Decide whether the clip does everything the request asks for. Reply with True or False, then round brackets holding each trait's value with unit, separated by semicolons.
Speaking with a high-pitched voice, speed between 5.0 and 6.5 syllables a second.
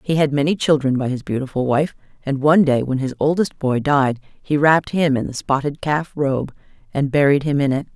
False (140 Hz; 5.4 syllables/s)